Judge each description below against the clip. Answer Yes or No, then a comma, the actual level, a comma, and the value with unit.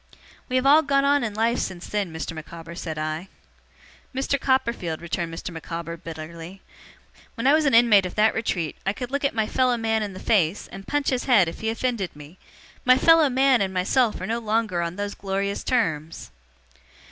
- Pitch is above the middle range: Yes, high, 210 Hz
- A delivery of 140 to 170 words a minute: No, average, 195 wpm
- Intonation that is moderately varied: No, wide, 6.8 semitones